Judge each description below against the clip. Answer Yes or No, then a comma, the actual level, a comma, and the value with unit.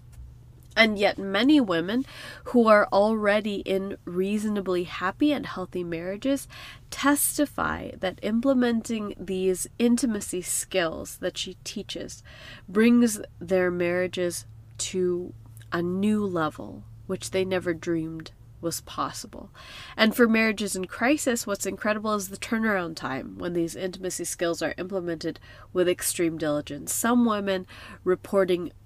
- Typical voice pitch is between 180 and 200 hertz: Yes, medium, 185 Hz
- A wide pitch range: No, average, 4.0 semitones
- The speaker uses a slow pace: Yes, slow, 120 wpm